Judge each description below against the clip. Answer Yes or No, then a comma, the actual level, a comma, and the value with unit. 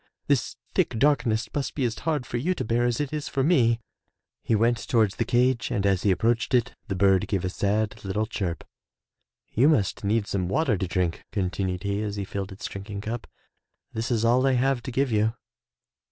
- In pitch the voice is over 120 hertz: No, low, 110 Hz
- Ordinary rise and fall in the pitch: Yes, average, 4.0 semitones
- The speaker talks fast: Yes, fast, 210 wpm